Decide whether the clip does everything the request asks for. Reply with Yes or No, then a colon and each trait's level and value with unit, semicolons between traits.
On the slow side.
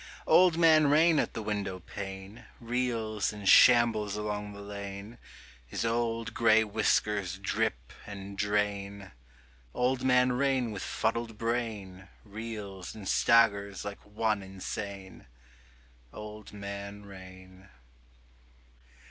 Yes: slow, 105 wpm